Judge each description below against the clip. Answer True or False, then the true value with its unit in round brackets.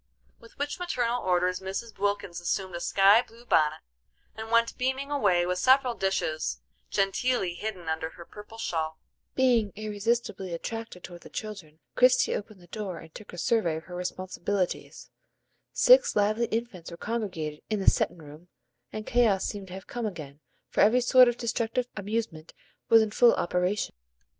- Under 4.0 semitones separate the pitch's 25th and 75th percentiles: False (4.7 semitones)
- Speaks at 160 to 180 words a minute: True (165 wpm)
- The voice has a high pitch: True (205 Hz)